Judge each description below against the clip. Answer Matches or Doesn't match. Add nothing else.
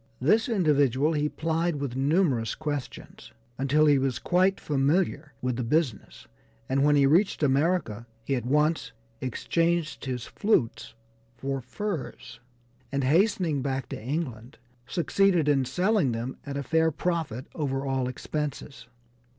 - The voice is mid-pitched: Matches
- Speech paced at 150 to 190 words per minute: Doesn't match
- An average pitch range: Matches